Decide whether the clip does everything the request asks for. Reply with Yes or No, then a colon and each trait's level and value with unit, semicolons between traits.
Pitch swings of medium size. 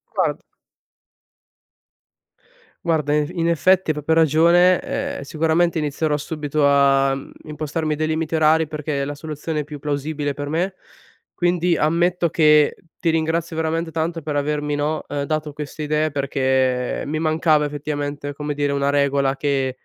No: narrow, 2.1 semitones